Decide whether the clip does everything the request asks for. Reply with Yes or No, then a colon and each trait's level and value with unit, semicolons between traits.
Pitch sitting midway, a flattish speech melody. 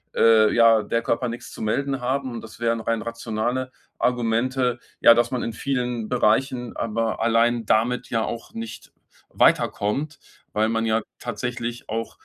No: low, 115 Hz; narrow, 1.6 semitones